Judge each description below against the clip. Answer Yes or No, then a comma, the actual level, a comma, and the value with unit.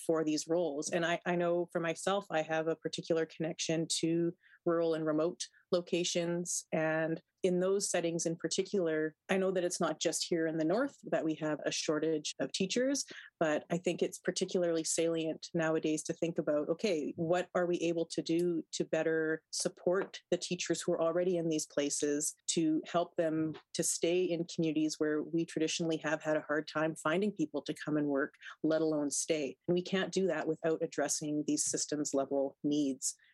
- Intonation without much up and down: Yes, narrow, 2.1 semitones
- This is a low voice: No, medium, 165 Hz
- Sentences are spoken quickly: No, average, 190 wpm